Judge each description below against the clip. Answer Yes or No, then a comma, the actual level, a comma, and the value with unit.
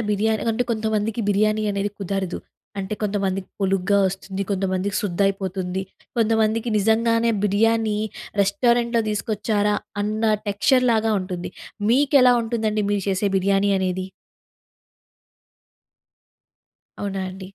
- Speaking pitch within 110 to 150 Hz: No, high, 205 Hz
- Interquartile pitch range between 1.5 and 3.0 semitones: Yes, narrow, 2.4 semitones